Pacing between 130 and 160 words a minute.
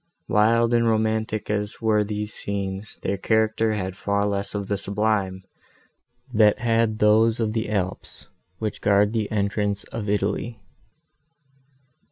Yes: slow, 135 wpm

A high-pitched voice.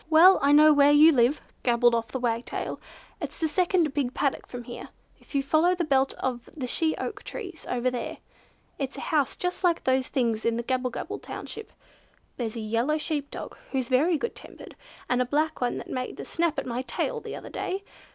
Yes: very high, 275 Hz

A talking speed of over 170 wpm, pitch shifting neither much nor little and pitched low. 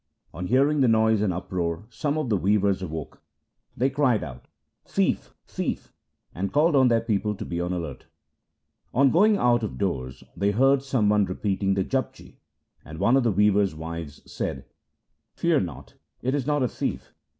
No: average, 190 wpm; wide, 6.5 semitones; low, 105 Hz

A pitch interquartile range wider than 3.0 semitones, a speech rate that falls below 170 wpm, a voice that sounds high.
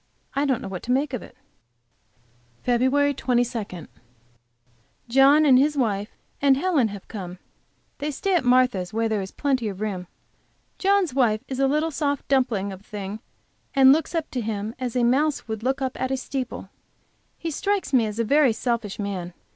No: average, 4.7 semitones; average, 175 wpm; very high, 250 Hz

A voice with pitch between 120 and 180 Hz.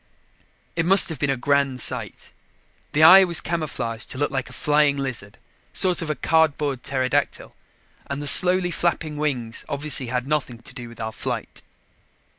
Yes: medium, 140 Hz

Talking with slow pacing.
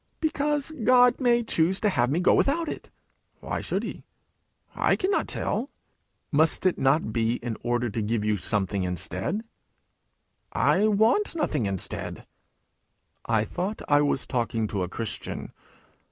No: average, 145 wpm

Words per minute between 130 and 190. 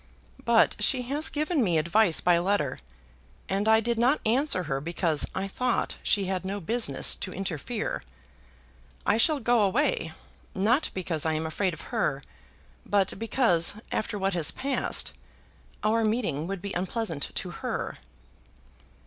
Yes: average, 150 wpm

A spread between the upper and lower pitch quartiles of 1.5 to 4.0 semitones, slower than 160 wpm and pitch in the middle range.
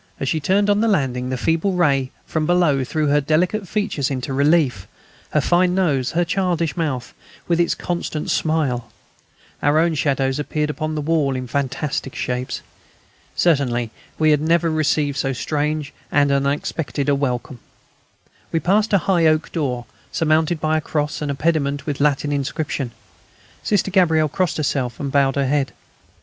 No: average, 3.2 semitones; average, 170 wpm; medium, 150 Hz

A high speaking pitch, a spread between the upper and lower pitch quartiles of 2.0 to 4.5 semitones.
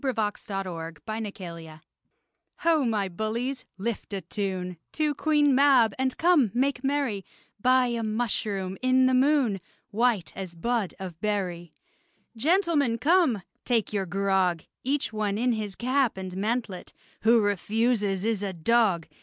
No: high, 220 Hz; average, 5.0 semitones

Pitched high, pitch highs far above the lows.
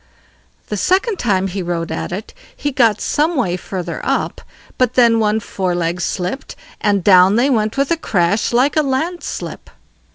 Yes: high, 215 Hz; wide, 6.4 semitones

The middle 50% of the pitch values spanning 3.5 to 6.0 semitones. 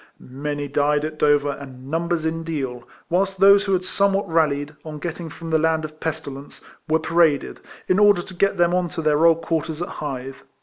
No: average, 3.0 semitones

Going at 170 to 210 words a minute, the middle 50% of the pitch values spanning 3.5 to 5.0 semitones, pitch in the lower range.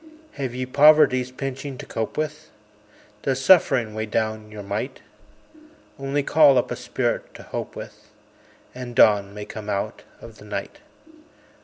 No: average, 150 wpm; average, 4.1 semitones; low, 125 Hz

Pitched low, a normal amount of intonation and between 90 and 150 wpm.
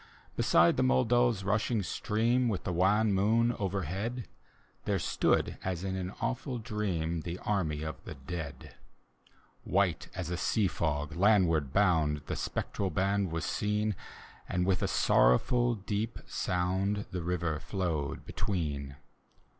Yes: very low, 95 Hz; average, 4.3 semitones; slow, 135 wpm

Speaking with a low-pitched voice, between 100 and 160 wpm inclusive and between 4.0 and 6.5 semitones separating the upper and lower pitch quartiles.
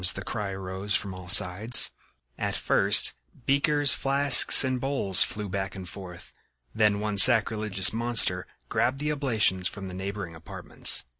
Yes: low, 105 Hz; average, 145 wpm; average, 4.5 semitones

